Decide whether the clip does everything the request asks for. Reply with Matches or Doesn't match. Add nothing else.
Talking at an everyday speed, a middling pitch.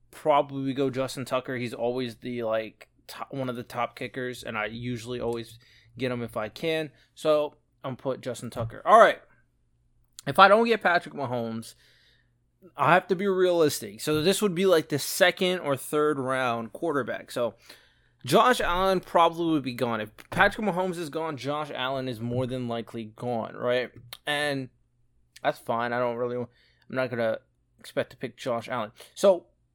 Doesn't match